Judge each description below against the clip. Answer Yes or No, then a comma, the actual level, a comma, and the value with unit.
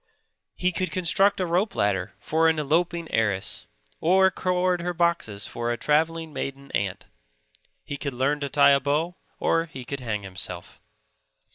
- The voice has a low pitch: No, medium, 150 Hz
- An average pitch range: No, wide, 5.7 semitones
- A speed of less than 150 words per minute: No, average, 160 wpm